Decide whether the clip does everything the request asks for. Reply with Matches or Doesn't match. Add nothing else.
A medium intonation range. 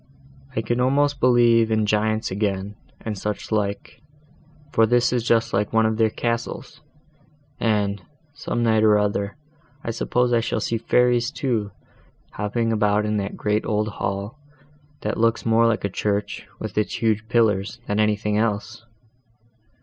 Doesn't match